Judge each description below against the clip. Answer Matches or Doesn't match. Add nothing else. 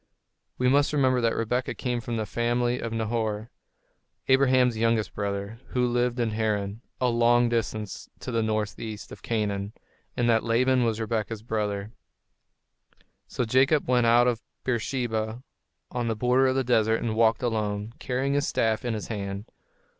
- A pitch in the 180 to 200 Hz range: Doesn't match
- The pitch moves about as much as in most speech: Doesn't match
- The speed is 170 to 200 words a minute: Doesn't match